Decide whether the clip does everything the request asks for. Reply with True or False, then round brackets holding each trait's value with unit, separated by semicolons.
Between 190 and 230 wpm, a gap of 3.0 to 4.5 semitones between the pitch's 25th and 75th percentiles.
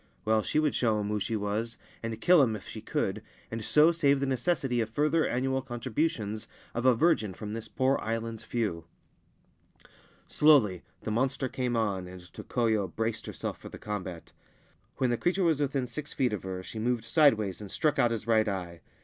True (195 wpm; 4.0 semitones)